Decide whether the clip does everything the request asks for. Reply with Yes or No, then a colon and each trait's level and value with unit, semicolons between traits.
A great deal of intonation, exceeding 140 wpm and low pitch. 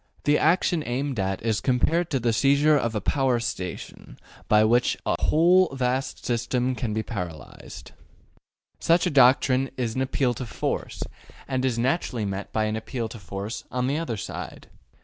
No: average, 3.8 semitones; average, 170 wpm; low, 125 Hz